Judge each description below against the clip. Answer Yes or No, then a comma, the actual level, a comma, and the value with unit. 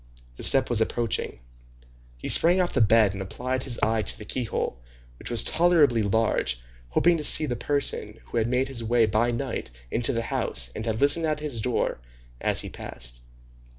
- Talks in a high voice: No, low, 115 Hz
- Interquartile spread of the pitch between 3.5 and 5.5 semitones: Yes, average, 3.9 semitones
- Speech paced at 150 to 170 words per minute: No, average, 190 wpm